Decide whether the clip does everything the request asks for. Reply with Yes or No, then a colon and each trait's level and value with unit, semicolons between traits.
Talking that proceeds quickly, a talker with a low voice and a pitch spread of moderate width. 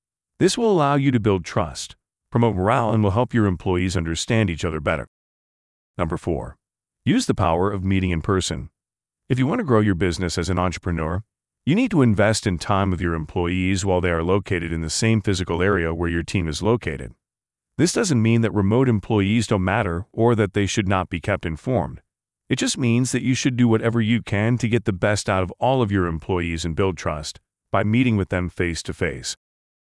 Yes: fast, 215 wpm; low, 100 Hz; average, 4.5 semitones